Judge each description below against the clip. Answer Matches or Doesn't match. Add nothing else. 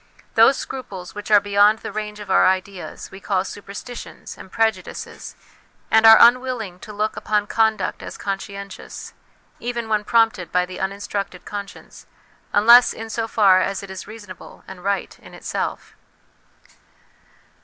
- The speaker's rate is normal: Matches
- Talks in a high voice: Matches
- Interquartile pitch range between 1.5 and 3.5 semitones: Matches